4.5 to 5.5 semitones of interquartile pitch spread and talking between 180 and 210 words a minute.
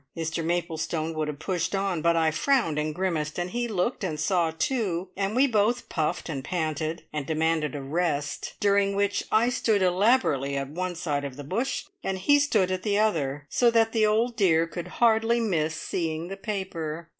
Yes: average, 5.1 semitones; average, 190 wpm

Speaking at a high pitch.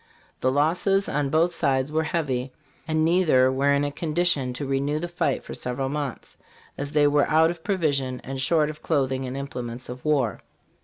No: medium, 145 Hz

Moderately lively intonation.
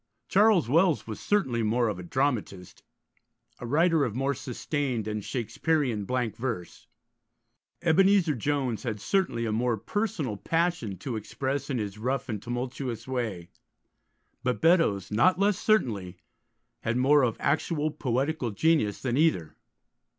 No: wide, 6.0 semitones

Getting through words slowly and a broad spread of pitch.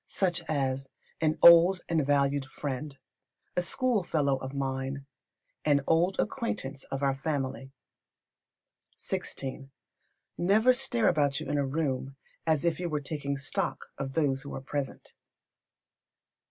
No: slow, 130 wpm; average, 3.7 semitones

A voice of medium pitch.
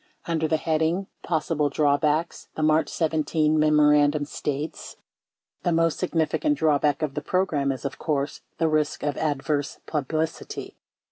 Yes: medium, 155 Hz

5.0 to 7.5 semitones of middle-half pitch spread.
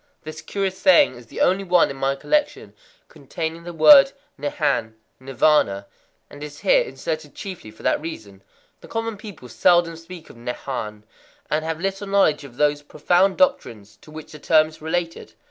Yes: wide, 5.5 semitones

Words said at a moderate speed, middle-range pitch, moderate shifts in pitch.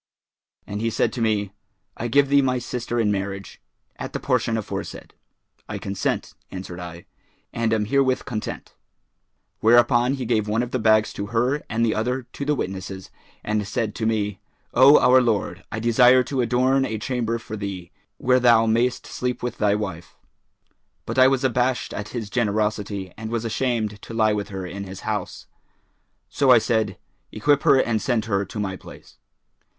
No: average, 180 wpm; low, 115 Hz; average, 3.2 semitones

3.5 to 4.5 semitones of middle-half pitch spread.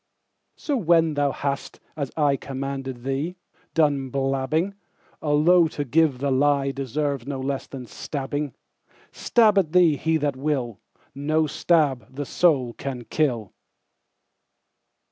No: average, 2.7 semitones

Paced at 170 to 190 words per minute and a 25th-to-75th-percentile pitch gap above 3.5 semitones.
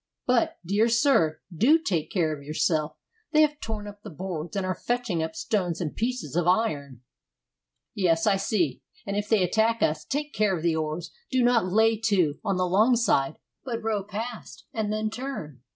Yes: average, 185 wpm; wide, 5.6 semitones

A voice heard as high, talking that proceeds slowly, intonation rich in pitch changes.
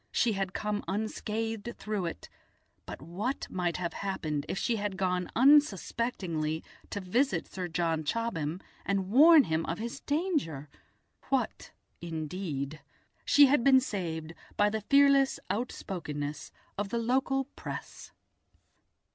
Yes: high, 195 Hz; slow, 130 wpm; wide, 6.1 semitones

